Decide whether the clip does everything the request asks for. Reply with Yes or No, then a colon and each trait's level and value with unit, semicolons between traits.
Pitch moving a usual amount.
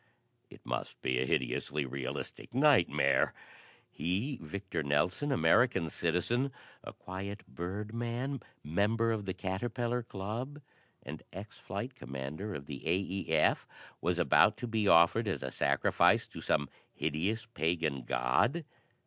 No: wide, 7.2 semitones